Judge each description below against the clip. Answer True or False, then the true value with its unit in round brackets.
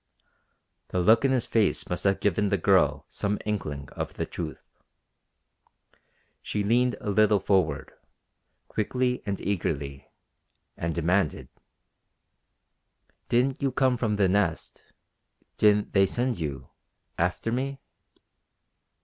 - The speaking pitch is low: True (105 Hz)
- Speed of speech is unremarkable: False (115 wpm)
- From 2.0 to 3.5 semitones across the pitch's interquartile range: False (5.1 semitones)